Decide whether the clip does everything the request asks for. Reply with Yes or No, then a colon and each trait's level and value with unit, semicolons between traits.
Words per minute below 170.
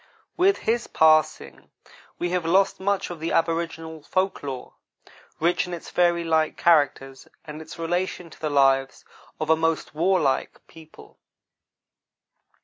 Yes: average, 140 wpm